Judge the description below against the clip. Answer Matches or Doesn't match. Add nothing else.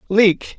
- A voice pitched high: Matches